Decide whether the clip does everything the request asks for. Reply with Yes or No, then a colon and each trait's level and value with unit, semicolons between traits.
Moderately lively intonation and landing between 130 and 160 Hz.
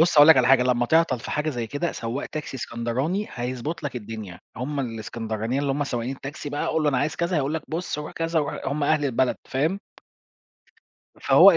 Yes: average, 4.1 semitones; medium, 140 Hz